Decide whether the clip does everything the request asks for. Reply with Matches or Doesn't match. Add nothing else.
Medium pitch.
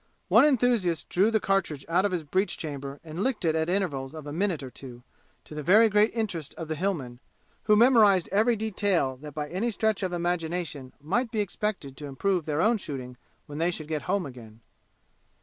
Matches